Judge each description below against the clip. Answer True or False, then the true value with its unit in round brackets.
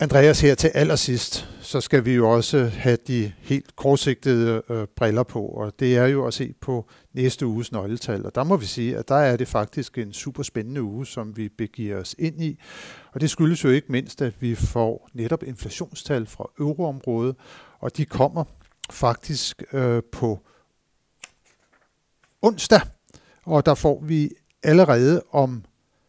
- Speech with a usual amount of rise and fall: True (3.8 semitones)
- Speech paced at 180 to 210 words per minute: False (165 wpm)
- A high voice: False (130 Hz)